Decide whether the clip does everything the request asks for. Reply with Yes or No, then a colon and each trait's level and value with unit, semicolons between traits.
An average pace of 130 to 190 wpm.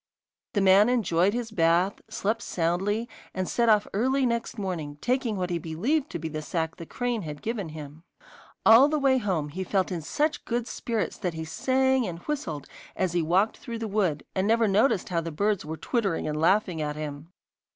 No: average, 200 wpm